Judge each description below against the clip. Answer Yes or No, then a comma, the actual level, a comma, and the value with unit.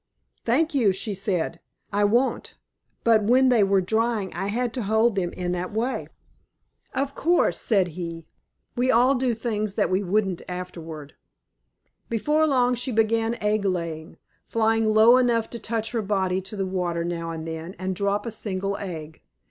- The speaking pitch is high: Yes, high, 210 Hz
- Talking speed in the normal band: Yes, average, 170 wpm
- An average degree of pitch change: Yes, average, 4.2 semitones